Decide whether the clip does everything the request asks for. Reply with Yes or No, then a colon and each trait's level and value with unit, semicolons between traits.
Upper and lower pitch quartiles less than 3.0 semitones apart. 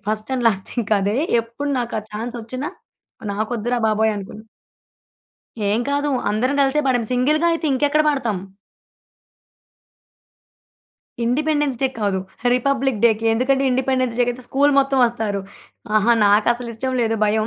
No: average, 3.7 semitones